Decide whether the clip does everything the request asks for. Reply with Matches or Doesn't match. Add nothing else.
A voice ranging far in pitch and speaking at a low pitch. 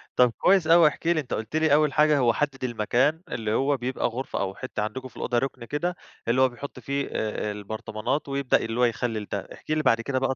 Doesn't match